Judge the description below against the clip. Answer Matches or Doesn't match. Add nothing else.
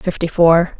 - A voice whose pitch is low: Doesn't match